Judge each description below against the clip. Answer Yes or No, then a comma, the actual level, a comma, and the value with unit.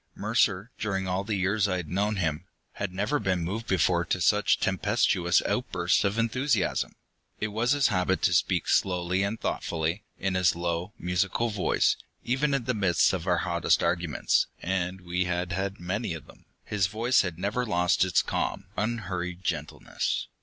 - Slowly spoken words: No, average, 170 wpm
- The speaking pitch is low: Yes, very low, 95 Hz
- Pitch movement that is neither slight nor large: Yes, average, 3.1 semitones